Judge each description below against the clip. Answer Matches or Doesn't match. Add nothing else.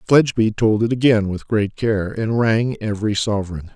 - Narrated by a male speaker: Matches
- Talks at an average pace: Matches